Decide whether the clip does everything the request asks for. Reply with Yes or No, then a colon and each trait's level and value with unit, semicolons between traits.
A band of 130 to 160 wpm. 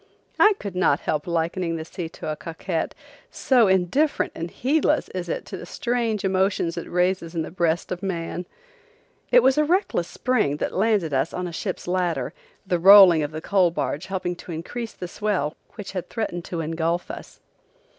No: average, 185 wpm